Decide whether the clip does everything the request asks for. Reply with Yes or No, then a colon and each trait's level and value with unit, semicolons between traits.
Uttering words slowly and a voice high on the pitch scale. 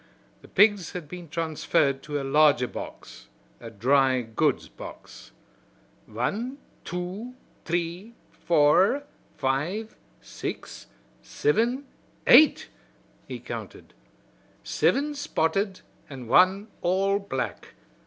No: slow, 95 wpm; medium, 175 Hz